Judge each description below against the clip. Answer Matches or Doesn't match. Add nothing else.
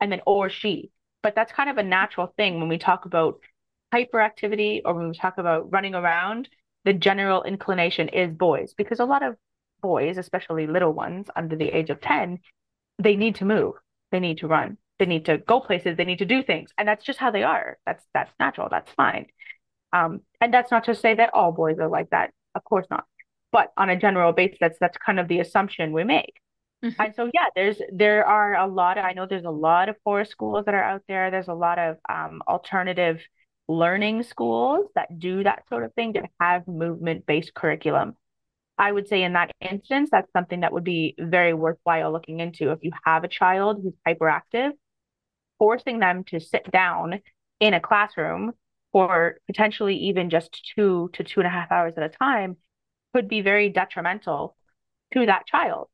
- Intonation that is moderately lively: Matches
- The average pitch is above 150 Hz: Matches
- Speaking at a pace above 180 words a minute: Matches